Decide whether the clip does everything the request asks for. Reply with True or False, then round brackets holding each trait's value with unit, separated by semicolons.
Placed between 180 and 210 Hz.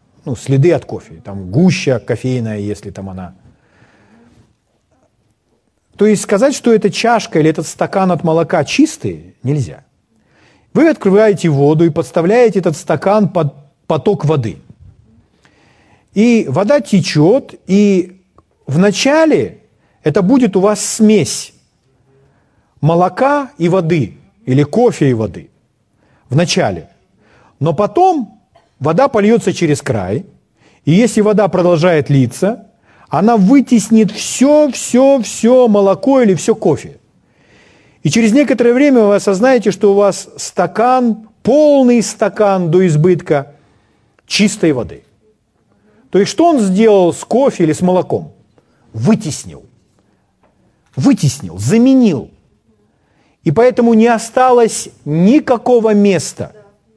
True (185 Hz)